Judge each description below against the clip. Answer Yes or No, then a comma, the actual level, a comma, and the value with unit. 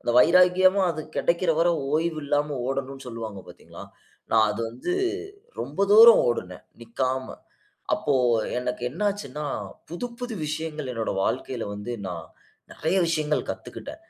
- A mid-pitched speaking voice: Yes, medium, 150 Hz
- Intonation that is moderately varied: No, wide, 6.1 semitones